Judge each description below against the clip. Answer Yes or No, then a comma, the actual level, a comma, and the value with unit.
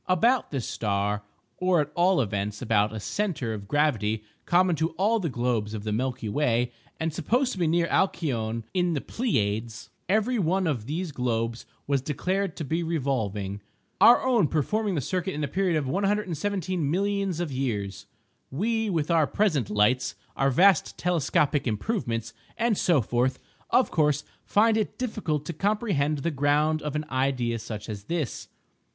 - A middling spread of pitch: No, wide, 7.6 semitones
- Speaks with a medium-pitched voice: Yes, medium, 150 Hz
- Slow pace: No, average, 165 wpm